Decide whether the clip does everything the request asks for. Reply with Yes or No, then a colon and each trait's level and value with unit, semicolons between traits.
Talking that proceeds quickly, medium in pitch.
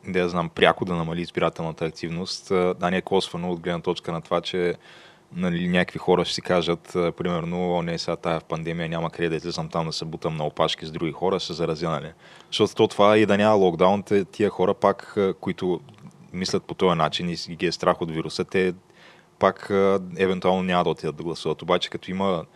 No: fast, 205 wpm; very low, 90 Hz